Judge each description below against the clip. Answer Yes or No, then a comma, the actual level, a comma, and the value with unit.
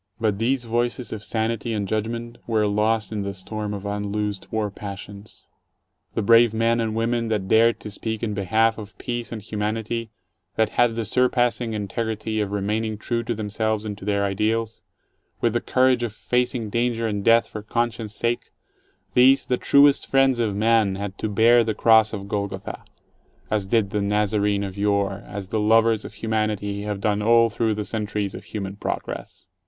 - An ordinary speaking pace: Yes, average, 180 wpm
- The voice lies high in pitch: No, low, 110 Hz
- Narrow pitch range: Yes, narrow, 2.1 semitones